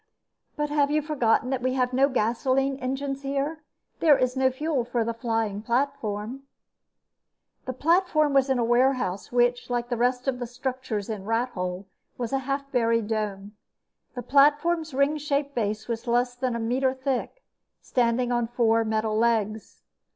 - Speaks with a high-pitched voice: Yes, very high, 250 Hz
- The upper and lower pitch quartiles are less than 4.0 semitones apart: Yes, average, 3.1 semitones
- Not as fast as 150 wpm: No, average, 165 wpm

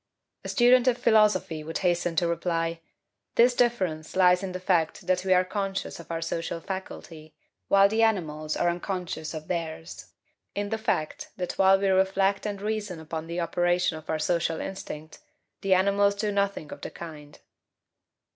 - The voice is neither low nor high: Yes, medium, 180 Hz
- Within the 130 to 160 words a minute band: No, average, 170 wpm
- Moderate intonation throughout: Yes, average, 3.3 semitones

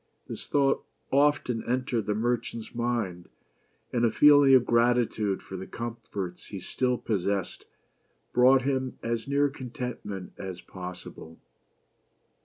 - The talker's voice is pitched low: Yes, low, 120 Hz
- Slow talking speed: Yes, slow, 120 wpm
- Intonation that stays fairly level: No, average, 4.3 semitones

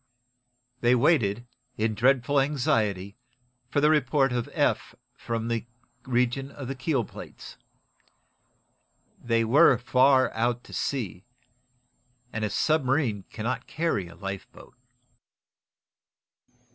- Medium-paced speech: No, slow, 110 wpm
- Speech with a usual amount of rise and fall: Yes, average, 3.6 semitones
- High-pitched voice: No, low, 120 Hz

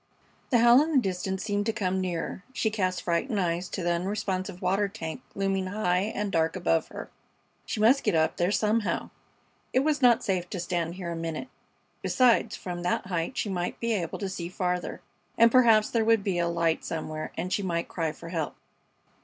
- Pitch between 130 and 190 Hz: Yes, medium, 185 Hz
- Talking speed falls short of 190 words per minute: No, average, 200 wpm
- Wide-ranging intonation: No, average, 3.8 semitones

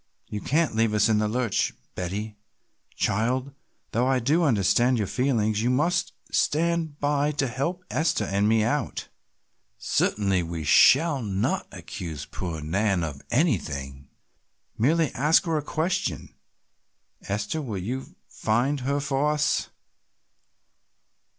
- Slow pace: Yes, slow, 130 wpm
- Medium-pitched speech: No, low, 120 Hz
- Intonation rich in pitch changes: Yes, wide, 6.3 semitones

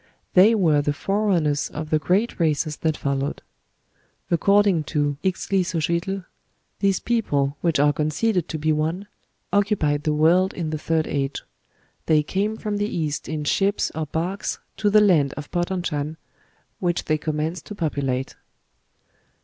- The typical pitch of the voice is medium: Yes, medium, 160 Hz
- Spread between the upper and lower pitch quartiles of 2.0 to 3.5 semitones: No, average, 4.3 semitones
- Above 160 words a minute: No, average, 150 wpm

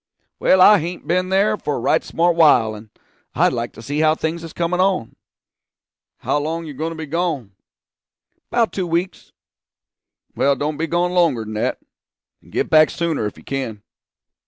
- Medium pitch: Yes, medium, 160 Hz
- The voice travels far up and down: No, average, 4.2 semitones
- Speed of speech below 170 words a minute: No, average, 185 wpm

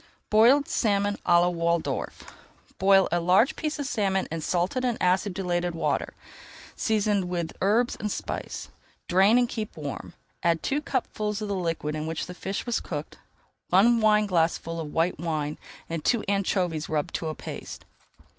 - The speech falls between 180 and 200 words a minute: No, average, 160 wpm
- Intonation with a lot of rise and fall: No, average, 4.2 semitones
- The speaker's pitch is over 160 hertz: Yes, medium, 185 Hz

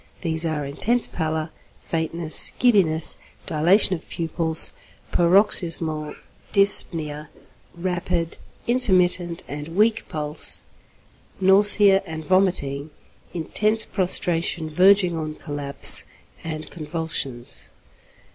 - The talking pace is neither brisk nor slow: No, slow, 85 wpm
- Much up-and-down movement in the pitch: No, average, 3.2 semitones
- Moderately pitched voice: Yes, medium, 165 Hz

